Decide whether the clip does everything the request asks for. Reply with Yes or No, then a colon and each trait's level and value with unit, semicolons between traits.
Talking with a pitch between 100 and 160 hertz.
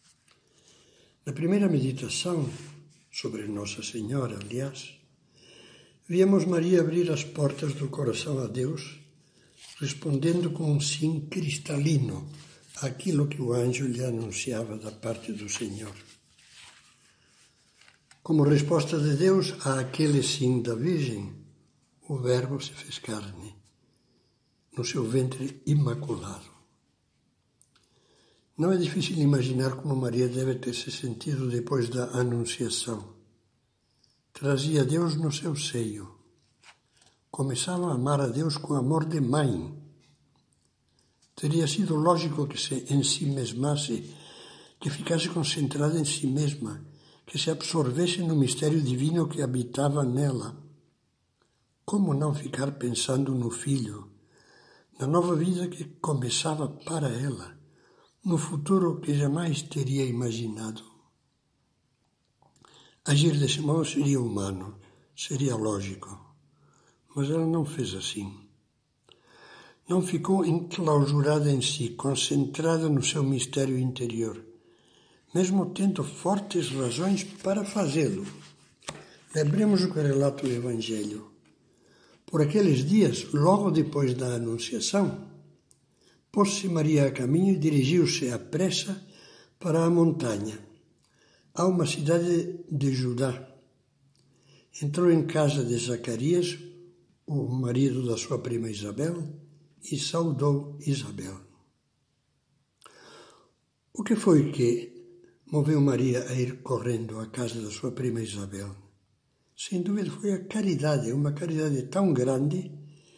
Yes: medium, 140 Hz